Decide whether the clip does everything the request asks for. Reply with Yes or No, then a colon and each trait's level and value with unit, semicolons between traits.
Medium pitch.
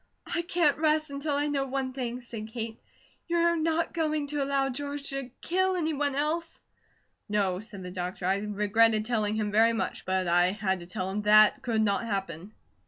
No: high, 235 Hz